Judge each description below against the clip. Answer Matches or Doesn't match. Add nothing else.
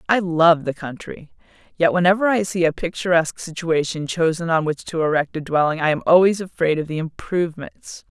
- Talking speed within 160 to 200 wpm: Matches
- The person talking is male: Doesn't match